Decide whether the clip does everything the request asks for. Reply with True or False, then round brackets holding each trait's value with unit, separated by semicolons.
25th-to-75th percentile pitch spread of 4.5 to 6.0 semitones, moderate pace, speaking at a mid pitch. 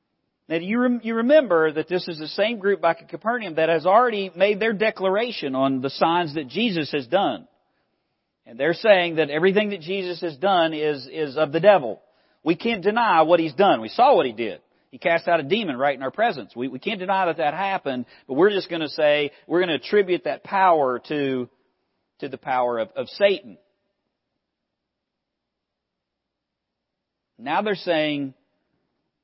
True (4.8 semitones; 185 wpm; 175 Hz)